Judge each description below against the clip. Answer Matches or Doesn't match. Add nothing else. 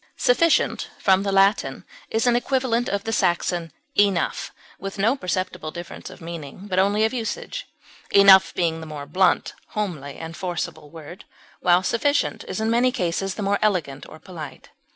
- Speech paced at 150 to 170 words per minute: Matches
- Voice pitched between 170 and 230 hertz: Matches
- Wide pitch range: Doesn't match